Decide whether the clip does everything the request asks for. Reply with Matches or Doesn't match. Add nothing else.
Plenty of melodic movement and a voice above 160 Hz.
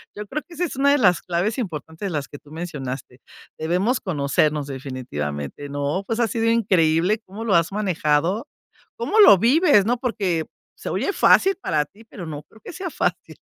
Matches